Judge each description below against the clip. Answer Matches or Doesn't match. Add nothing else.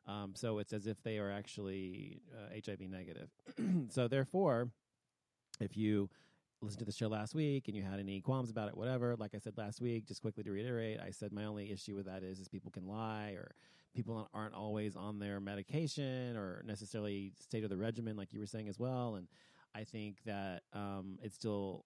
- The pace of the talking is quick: Matches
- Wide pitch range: Doesn't match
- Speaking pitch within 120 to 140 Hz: Doesn't match